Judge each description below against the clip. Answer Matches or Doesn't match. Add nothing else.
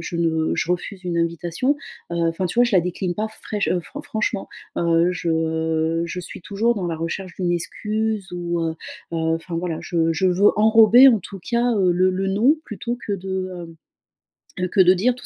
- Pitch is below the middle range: Doesn't match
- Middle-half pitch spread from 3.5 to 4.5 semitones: Matches